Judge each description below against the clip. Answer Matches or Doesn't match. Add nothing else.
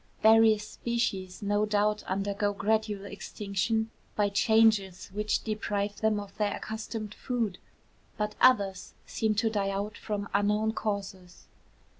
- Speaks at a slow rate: Matches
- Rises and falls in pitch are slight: Matches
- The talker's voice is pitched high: Matches